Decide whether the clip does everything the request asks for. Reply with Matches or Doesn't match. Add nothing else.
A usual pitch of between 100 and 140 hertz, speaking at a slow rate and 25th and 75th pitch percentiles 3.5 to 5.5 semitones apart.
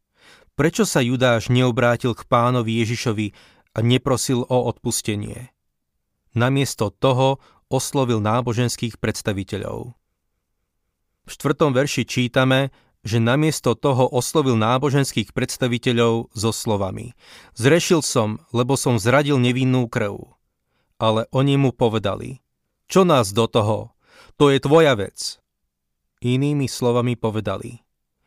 Doesn't match